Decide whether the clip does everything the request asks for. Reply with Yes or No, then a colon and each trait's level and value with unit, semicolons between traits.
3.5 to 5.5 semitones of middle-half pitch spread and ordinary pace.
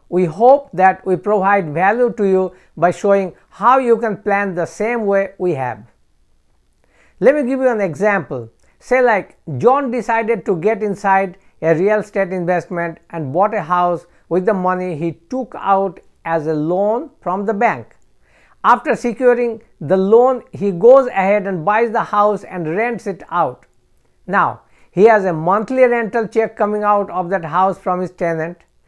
Yes: average, 4.2 semitones; average, 170 wpm